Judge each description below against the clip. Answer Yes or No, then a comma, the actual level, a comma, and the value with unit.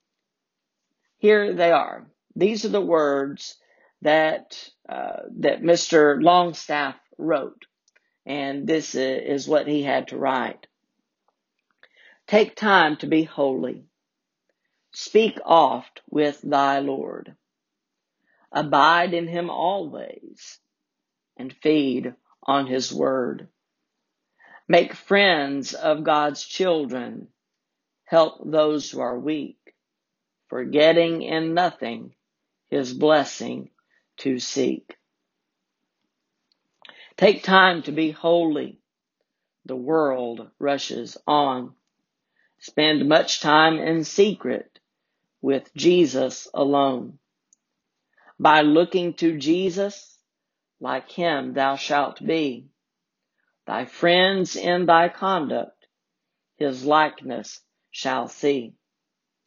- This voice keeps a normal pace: No, slow, 95 wpm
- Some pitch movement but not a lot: Yes, average, 3.6 semitones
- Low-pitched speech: No, medium, 155 Hz